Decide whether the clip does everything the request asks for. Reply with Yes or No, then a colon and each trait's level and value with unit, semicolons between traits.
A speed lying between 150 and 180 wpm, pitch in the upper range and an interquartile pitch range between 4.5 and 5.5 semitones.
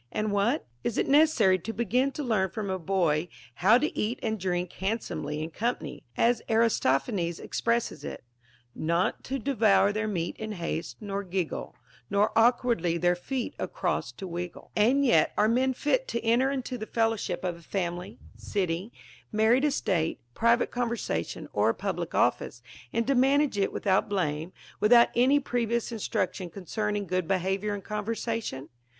Yes: average, 170 wpm; high, 210 Hz; average, 4.8 semitones